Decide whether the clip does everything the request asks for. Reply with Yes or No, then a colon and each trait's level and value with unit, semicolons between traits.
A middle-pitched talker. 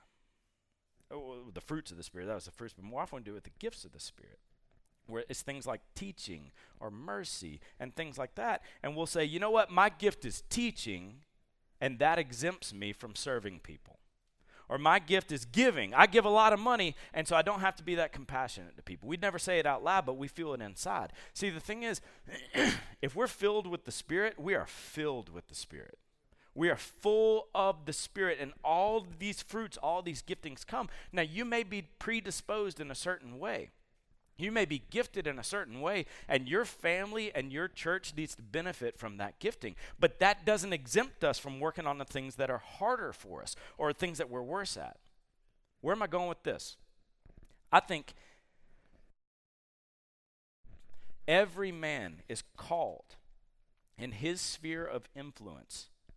Yes: medium, 160 Hz